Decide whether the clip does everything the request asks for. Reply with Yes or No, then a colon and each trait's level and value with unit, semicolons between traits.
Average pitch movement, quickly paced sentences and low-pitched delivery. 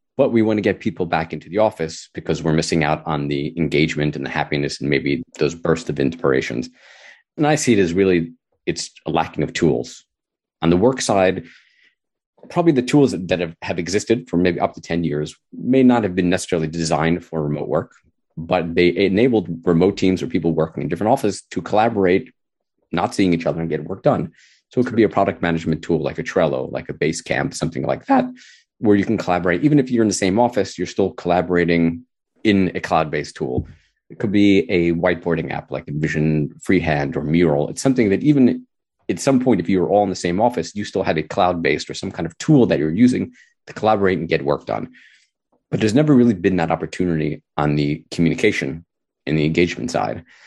Yes: average, 4.7 semitones; fast, 215 wpm; very low, 90 Hz